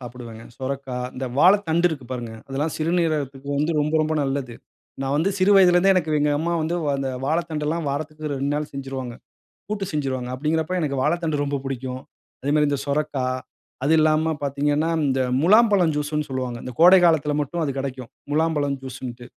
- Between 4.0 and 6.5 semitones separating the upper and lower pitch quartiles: No, average, 3.1 semitones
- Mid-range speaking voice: Yes, medium, 150 Hz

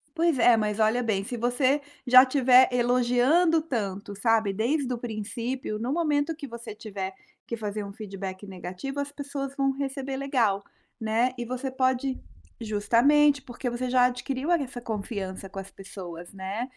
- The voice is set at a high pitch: Yes, high, 245 Hz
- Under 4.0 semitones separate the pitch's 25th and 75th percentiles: No, average, 4.3 semitones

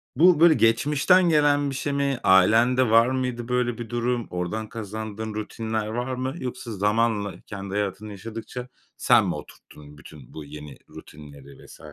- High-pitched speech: No, low, 115 Hz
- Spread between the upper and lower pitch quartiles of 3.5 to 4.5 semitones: Yes, average, 4.0 semitones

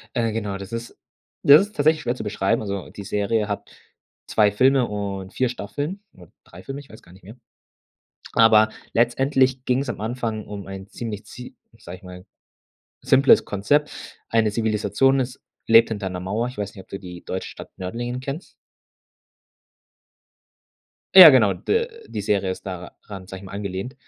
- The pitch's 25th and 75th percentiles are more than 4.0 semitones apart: Yes, average, 4.5 semitones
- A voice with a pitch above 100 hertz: Yes, low, 110 Hz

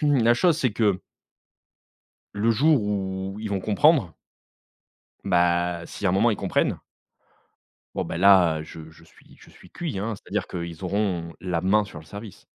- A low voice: Yes, very low, 95 Hz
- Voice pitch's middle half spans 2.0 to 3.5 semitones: No, average, 3.9 semitones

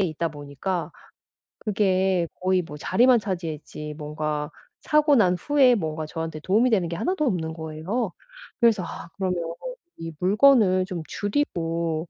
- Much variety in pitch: No, average, 4.7 semitones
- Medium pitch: Yes, medium, 180 Hz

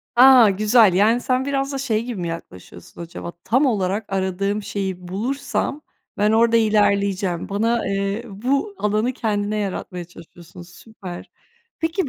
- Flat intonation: No, average, 4.0 semitones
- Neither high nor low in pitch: No, high, 210 Hz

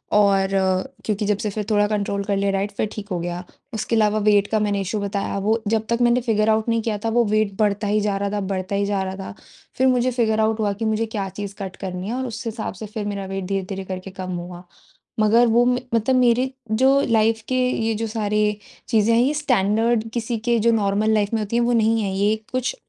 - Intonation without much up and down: Yes, narrow, 2.3 semitones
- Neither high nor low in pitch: No, high, 215 Hz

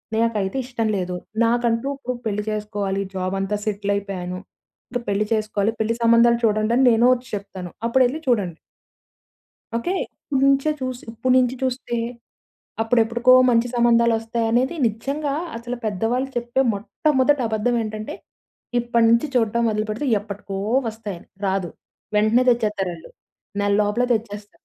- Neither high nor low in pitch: No, high, 225 Hz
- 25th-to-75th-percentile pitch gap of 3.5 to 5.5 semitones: No, average, 2.7 semitones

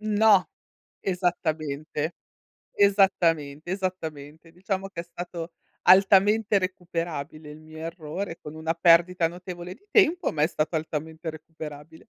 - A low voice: No, medium, 170 Hz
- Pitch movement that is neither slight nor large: Yes, average, 3.1 semitones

